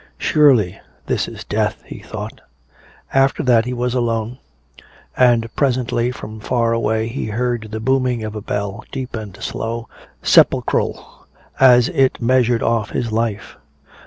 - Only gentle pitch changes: Yes, narrow, 2.2 semitones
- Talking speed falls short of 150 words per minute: Yes, average, 140 wpm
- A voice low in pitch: Yes, low, 115 Hz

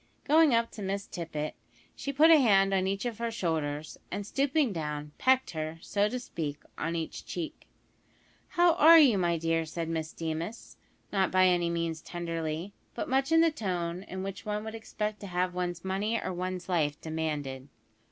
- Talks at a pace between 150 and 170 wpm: No, average, 185 wpm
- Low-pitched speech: No, medium, 185 Hz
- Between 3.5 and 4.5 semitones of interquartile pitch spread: No, average, 5.2 semitones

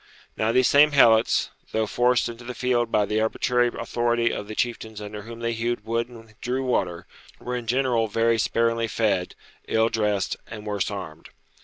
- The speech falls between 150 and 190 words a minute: Yes, average, 180 wpm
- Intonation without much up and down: Yes, narrow, 1.9 semitones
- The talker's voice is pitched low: Yes, low, 115 Hz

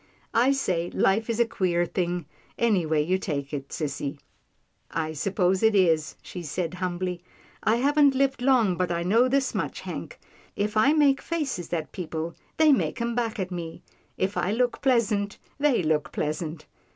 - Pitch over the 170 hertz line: Yes, high, 190 Hz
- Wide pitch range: Yes, wide, 5.9 semitones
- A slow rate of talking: No, average, 175 wpm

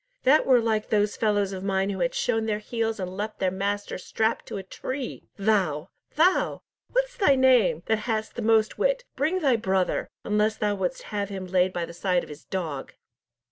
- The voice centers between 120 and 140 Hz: No, high, 210 Hz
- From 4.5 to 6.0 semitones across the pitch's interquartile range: No, average, 3.3 semitones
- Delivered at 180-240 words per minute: Yes, average, 200 wpm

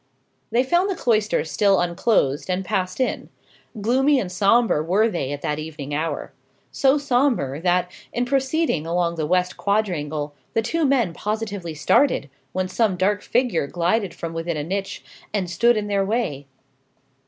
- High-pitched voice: Yes, high, 195 Hz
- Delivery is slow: No, average, 165 wpm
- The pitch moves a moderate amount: No, wide, 6.0 semitones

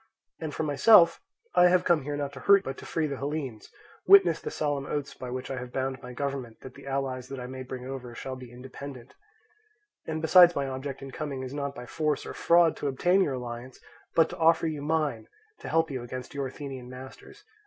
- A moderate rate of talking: No, fast, 220 wpm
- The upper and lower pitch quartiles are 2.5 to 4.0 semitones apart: Yes, average, 3.4 semitones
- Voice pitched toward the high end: No, medium, 140 Hz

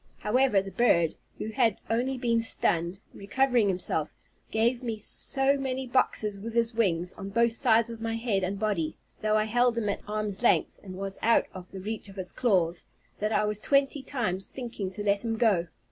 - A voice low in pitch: No, high, 215 Hz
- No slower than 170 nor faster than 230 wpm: Yes, average, 195 wpm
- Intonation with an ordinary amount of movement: Yes, average, 3.4 semitones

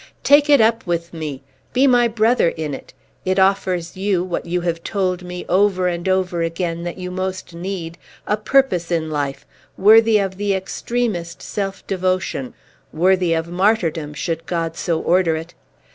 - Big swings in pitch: No, average, 2.9 semitones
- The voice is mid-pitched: Yes, medium, 180 Hz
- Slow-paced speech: No, average, 165 wpm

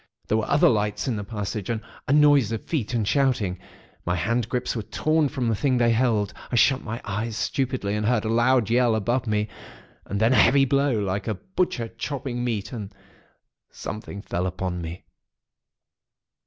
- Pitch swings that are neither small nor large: Yes, average, 3.7 semitones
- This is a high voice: No, low, 115 Hz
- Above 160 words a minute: Yes, average, 185 wpm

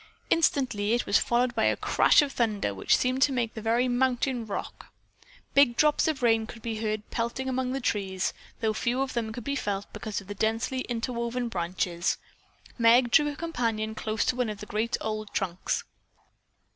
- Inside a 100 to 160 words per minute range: No, average, 190 wpm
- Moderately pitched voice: No, high, 235 Hz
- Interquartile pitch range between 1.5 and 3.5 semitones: Yes, average, 2.9 semitones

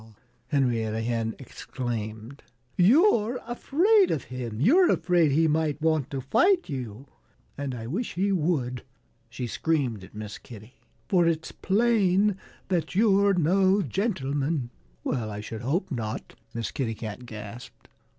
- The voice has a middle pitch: Yes, medium, 145 Hz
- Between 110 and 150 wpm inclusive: Yes, slow, 135 wpm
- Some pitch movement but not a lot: No, wide, 8.1 semitones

